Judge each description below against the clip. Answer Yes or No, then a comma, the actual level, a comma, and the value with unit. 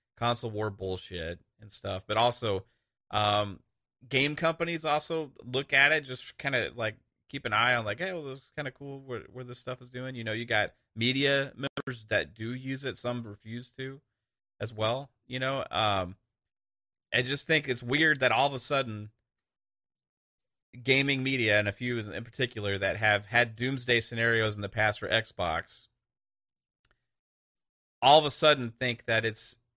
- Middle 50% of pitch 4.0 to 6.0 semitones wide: No, average, 3.6 semitones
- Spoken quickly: No, average, 180 wpm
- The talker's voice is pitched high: No, low, 120 Hz